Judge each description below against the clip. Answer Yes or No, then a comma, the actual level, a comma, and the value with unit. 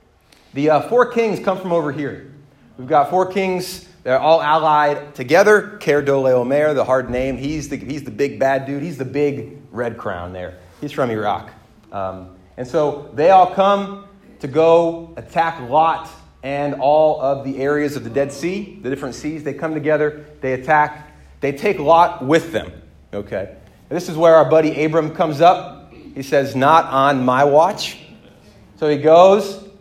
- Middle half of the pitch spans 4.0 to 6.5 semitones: No, average, 3.6 semitones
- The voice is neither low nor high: Yes, medium, 150 Hz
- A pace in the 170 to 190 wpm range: Yes, average, 175 wpm